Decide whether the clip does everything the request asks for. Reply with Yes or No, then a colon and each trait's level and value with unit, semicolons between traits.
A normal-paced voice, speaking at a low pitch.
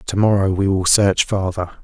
Yes: average, 195 wpm; very low, 95 Hz